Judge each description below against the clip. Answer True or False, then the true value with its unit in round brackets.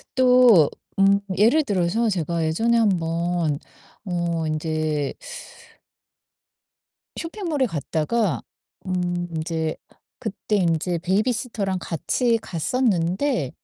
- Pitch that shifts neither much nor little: False (5.8 semitones)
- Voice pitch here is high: False (180 Hz)